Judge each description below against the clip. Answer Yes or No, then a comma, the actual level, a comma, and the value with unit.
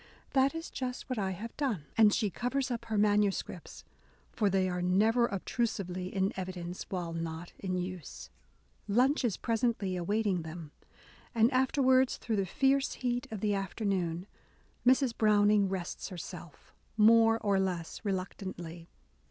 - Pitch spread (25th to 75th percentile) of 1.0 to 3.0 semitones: No, average, 4.3 semitones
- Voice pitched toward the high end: Yes, high, 205 Hz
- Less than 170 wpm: Yes, average, 155 wpm